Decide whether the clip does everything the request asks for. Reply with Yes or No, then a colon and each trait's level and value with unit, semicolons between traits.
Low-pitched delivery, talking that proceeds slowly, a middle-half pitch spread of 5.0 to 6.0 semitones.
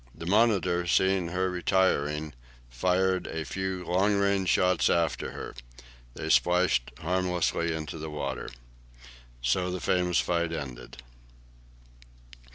No: very low, 90 Hz; slow, 115 wpm; average, 2.7 semitones